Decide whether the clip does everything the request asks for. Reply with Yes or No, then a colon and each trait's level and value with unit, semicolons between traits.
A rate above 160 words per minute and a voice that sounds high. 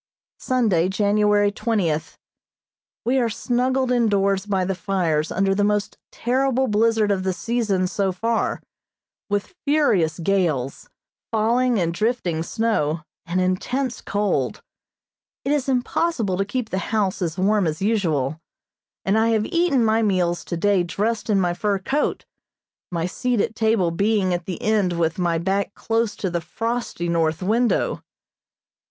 No: average, 145 wpm; high, 205 Hz